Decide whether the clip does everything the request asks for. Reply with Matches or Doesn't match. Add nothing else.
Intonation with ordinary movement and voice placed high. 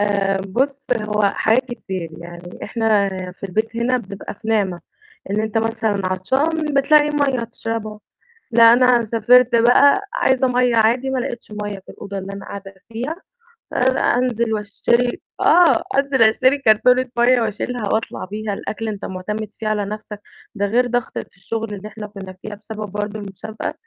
Matches